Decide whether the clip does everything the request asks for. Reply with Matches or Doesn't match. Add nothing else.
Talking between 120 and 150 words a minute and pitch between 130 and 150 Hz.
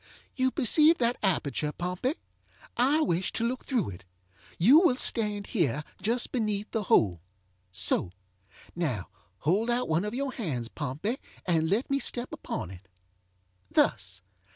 Doesn't match